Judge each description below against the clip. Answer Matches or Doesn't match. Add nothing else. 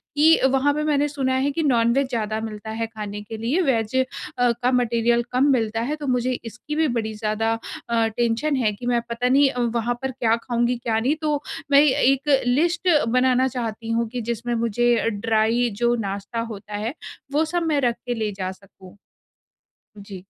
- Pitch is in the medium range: Doesn't match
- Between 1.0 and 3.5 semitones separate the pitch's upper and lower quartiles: Matches